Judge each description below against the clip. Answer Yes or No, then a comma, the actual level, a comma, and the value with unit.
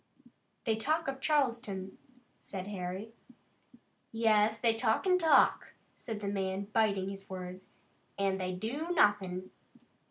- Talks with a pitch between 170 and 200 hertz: No, high, 210 Hz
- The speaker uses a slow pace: Yes, slow, 125 wpm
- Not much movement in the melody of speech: No, average, 3.5 semitones